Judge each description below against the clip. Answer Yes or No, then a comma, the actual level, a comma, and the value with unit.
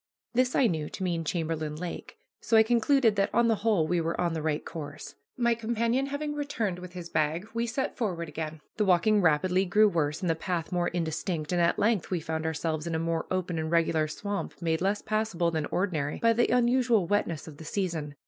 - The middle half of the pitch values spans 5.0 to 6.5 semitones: Yes, average, 5.3 semitones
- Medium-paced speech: No, fast, 215 wpm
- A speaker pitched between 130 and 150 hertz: No, medium, 175 Hz